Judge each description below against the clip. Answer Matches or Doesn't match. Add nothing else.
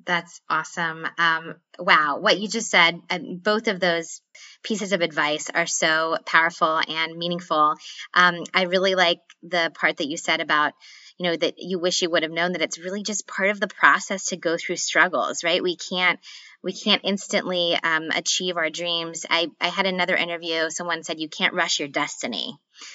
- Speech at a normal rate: Matches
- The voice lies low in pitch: Doesn't match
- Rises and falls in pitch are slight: Matches